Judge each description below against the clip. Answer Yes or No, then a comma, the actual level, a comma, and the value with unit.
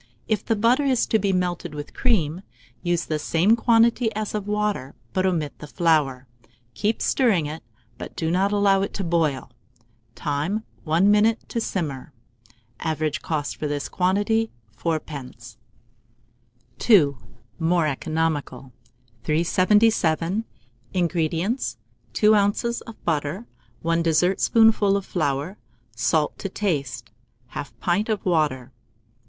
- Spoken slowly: Yes, slow, 125 wpm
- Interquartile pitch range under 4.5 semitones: No, average, 5.3 semitones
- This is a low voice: No, medium, 175 Hz